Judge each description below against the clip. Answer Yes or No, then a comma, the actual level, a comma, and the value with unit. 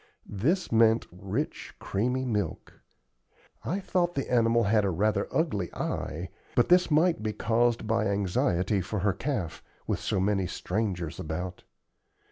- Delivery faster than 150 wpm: No, average, 140 wpm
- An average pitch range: Yes, average, 4.4 semitones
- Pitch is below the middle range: Yes, low, 105 Hz